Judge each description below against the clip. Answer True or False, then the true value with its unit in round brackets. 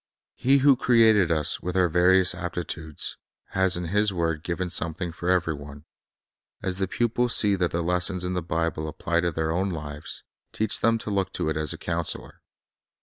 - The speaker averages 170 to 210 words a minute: True (190 wpm)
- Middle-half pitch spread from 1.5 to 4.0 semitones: True (2.7 semitones)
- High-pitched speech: False (90 Hz)